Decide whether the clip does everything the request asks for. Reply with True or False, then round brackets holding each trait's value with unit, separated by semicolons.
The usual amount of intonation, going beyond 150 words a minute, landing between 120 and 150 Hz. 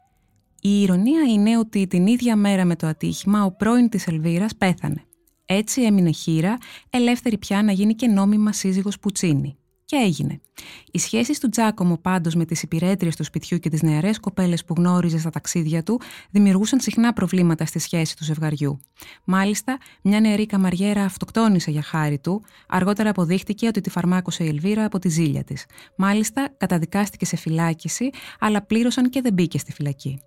False (4.2 semitones; 165 wpm; 190 Hz)